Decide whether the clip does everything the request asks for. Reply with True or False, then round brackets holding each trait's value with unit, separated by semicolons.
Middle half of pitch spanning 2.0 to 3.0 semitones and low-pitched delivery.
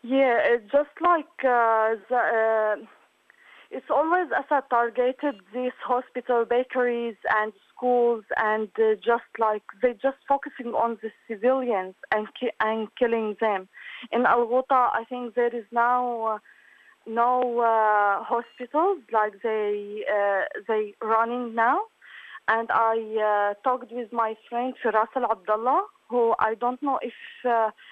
False (2.4 semitones; 235 Hz)